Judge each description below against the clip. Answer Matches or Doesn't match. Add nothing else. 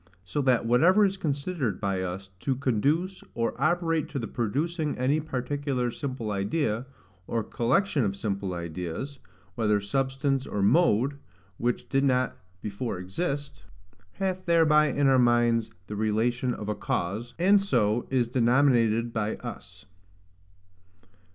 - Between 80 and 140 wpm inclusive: Matches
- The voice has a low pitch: Matches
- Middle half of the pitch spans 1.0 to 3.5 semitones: Doesn't match